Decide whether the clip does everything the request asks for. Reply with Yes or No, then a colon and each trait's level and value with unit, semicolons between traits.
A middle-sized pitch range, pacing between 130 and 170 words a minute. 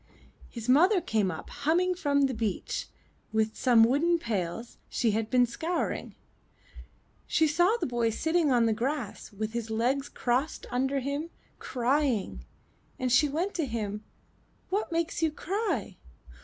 No: wide, 5.9 semitones; average, 145 wpm